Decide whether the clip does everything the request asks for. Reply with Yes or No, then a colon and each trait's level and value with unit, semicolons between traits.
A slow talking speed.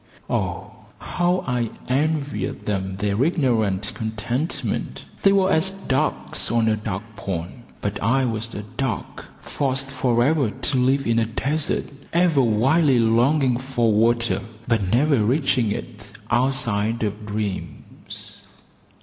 Yes: slow, 130 wpm